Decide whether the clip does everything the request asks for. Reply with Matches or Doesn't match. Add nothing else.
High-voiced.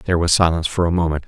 Doesn't match